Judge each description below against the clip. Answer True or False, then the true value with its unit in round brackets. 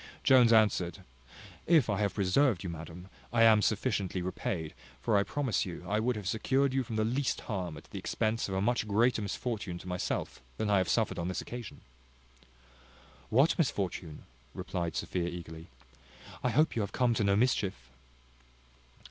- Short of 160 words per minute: False (175 wpm)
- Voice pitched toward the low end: True (105 Hz)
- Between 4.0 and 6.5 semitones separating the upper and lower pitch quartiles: True (4.7 semitones)